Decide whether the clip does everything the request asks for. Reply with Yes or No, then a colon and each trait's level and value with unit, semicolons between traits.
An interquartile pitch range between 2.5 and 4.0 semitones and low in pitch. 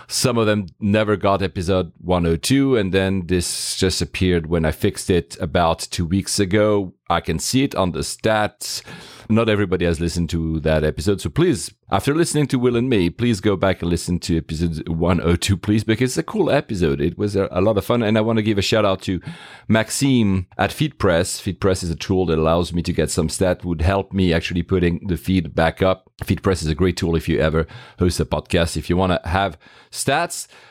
Yes: average, 3.5 semitones; very low, 95 Hz